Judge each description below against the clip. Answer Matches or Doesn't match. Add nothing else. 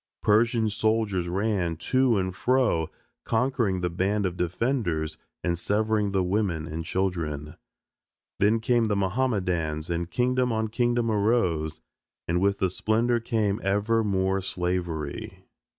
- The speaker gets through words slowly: Matches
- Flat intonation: Doesn't match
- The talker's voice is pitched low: Matches